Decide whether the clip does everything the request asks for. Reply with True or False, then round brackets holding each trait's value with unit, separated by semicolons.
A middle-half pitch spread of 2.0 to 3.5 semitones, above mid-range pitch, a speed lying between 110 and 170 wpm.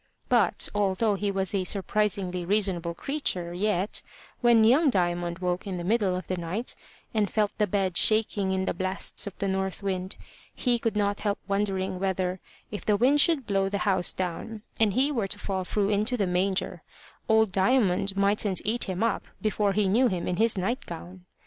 False (2.4 semitones; 200 Hz; 190 wpm)